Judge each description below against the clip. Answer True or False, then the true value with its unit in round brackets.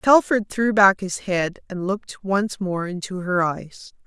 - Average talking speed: True (175 wpm)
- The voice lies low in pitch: False (195 Hz)